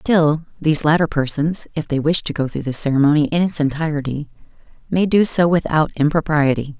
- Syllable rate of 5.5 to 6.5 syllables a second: Yes, 5.6 syllables/s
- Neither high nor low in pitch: Yes, medium, 155 Hz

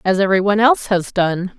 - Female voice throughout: Yes, female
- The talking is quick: No, average, 190 wpm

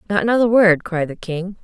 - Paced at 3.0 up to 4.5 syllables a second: No, 5.7 syllables/s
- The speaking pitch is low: No, high, 190 Hz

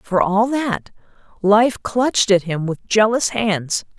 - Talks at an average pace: Yes, average, 150 wpm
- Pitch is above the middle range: Yes, high, 210 Hz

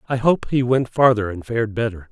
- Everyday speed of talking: No, fast, 225 wpm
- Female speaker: No, male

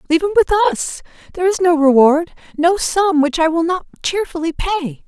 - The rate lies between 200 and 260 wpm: No, average, 190 wpm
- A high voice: Yes, very high, 335 Hz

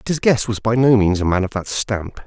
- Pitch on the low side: Yes, low, 110 Hz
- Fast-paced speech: Yes, fast, 320 wpm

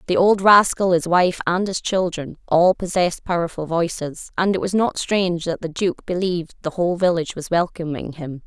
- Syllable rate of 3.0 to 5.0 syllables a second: No, 5.3 syllables/s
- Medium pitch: Yes, medium, 175 Hz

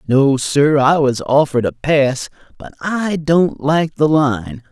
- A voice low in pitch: No, medium, 145 Hz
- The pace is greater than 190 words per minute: No, average, 165 wpm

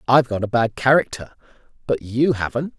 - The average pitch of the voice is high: No, low, 120 Hz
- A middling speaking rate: Yes, average, 170 wpm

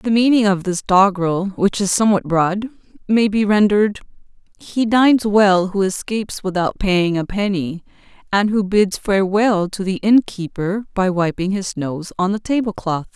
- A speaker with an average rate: Yes, average, 155 wpm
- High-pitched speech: Yes, high, 200 Hz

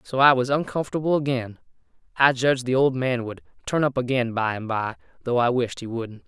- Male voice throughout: Yes, male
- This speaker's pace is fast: Yes, fast, 210 wpm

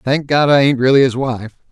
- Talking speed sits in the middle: No, fast, 245 wpm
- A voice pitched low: Yes, low, 130 Hz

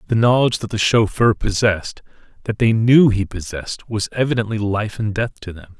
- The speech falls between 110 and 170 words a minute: No, average, 185 wpm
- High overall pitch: No, low, 110 Hz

